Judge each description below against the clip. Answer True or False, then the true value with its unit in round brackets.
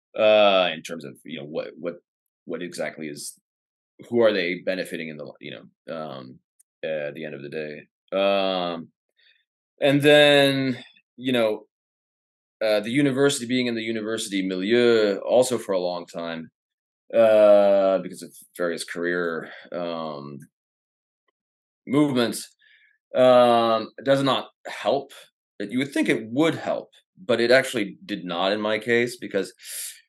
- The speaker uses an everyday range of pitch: False (6.6 semitones)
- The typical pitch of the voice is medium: False (105 Hz)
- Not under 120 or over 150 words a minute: True (140 wpm)